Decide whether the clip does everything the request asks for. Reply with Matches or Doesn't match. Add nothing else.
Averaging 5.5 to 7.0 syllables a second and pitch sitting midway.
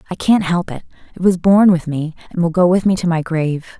Matches